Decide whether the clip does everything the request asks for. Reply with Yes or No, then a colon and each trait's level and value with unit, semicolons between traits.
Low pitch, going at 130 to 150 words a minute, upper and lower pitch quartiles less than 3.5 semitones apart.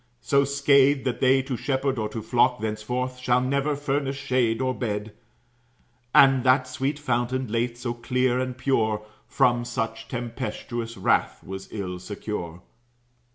Yes: low, 125 Hz; average, 145 wpm; average, 2.8 semitones